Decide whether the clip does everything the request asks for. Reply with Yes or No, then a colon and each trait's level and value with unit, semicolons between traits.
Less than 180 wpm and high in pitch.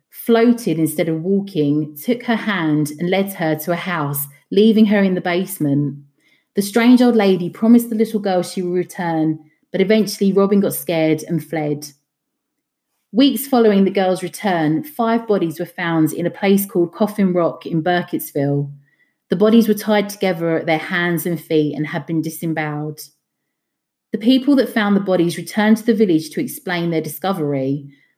No: average, 170 wpm; medium, 175 Hz